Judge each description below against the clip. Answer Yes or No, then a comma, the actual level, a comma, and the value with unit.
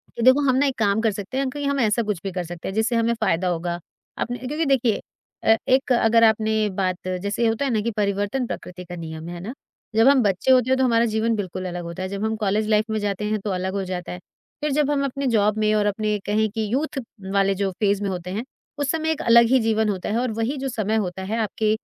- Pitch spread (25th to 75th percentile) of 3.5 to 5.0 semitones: Yes, average, 4.0 semitones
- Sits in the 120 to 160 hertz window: No, high, 215 Hz